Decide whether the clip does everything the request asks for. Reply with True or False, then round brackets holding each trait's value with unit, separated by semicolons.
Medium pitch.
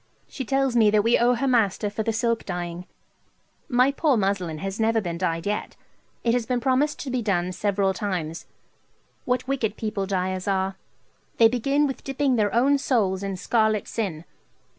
False (220 Hz)